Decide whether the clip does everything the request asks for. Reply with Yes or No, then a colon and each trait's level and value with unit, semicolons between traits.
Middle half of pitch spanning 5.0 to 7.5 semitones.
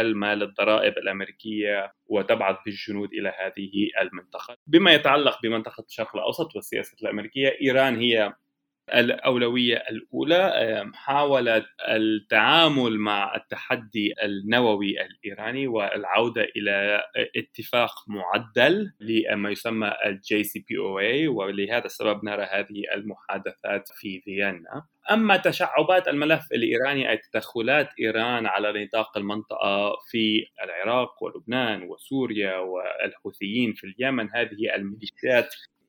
No: average, 3.1 semitones